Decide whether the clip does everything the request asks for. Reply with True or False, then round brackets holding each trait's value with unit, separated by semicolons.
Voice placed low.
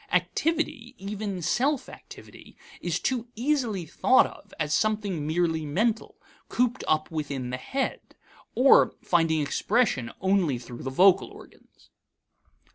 False (190 Hz)